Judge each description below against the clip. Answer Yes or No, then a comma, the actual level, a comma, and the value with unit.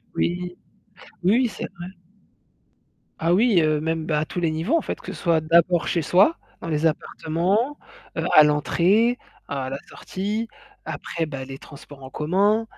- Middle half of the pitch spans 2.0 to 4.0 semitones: No, average, 4.5 semitones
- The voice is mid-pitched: Yes, medium, 170 Hz